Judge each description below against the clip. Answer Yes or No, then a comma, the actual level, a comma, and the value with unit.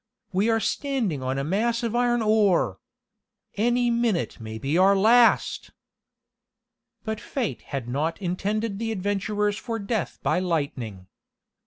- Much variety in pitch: Yes, wide, 5.7 semitones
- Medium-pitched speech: No, high, 205 Hz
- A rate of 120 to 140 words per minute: Yes, slow, 135 wpm